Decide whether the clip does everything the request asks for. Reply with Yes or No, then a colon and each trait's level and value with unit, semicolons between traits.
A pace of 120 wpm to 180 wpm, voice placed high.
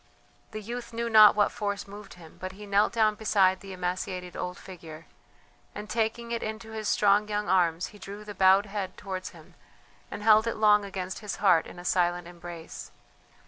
No: average, 190 wpm; high, 200 Hz